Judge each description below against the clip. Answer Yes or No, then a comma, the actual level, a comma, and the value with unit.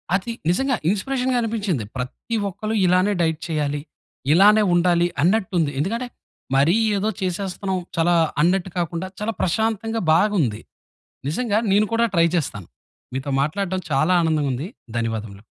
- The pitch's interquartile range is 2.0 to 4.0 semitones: No, average, 5.1 semitones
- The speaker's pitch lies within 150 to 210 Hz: Yes, medium, 185 Hz